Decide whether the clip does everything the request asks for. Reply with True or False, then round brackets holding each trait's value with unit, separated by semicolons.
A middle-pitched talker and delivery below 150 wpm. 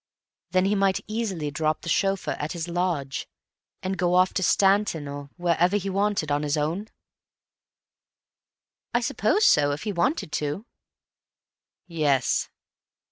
True (175 Hz; 135 wpm)